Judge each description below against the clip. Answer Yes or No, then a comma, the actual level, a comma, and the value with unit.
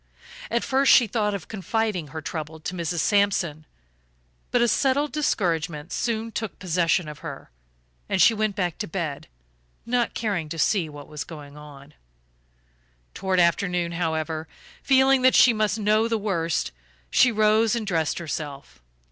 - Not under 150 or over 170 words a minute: Yes, average, 155 wpm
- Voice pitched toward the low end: No, medium, 185 Hz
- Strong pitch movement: Yes, wide, 5.8 semitones